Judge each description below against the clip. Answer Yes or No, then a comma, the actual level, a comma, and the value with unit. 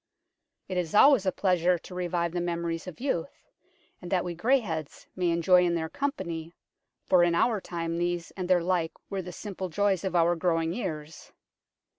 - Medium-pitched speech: Yes, medium, 175 Hz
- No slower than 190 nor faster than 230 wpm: No, average, 180 wpm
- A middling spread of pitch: No, narrow, 1.9 semitones